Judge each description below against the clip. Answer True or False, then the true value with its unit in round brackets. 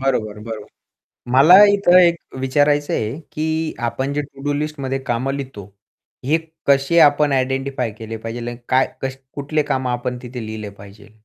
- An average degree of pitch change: True (3.4 semitones)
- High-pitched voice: False (135 Hz)